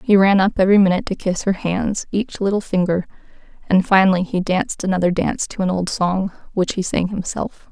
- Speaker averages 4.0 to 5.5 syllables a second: No, 5.7 syllables/s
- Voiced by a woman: Yes, female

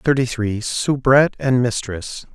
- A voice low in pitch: Yes, low, 125 Hz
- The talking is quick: No, slow, 130 wpm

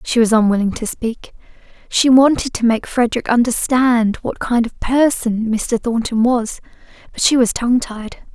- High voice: Yes, high, 235 Hz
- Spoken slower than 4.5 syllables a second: No, 4.6 syllables/s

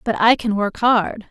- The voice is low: No, high, 215 Hz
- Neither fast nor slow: No, fast, 230 wpm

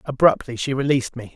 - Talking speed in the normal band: Yes, average, 175 wpm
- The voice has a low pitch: Yes, low, 130 Hz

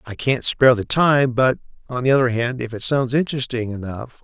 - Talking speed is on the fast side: Yes, fast, 210 wpm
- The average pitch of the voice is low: Yes, low, 125 Hz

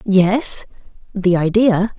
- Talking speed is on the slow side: Yes, slow, 90 wpm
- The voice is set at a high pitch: Yes, high, 200 Hz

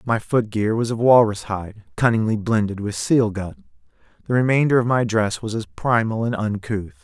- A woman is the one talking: No, male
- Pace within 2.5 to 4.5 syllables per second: No, 5.0 syllables/s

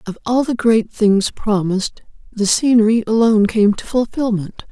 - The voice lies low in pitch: No, high, 220 Hz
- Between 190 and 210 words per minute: No, average, 155 wpm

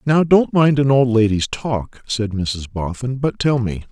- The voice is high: No, low, 120 Hz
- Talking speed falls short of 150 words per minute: No, average, 200 wpm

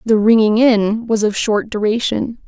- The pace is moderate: Yes, average, 170 wpm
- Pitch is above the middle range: Yes, high, 220 Hz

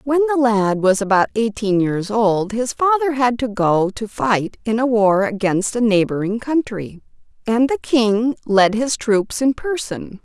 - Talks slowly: No, average, 175 wpm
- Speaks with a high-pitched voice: Yes, high, 225 Hz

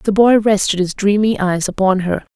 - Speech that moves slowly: No, fast, 205 wpm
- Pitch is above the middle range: Yes, high, 200 Hz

